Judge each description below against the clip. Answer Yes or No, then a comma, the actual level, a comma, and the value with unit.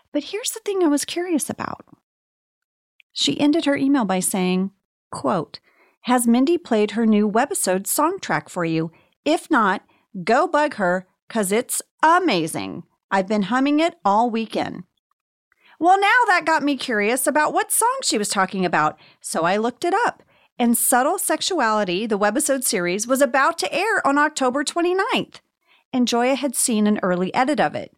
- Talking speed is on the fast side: No, average, 165 wpm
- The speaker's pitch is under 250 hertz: No, very high, 255 Hz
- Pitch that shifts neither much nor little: No, wide, 7.4 semitones